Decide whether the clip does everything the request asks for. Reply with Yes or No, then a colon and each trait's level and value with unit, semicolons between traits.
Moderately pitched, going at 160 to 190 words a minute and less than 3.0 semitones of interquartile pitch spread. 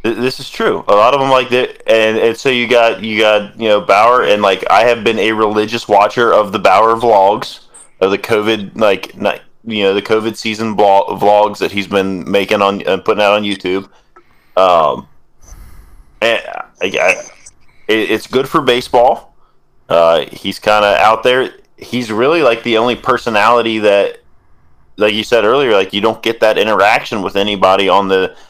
No: low, 105 Hz; average, 185 wpm; narrow, 2.4 semitones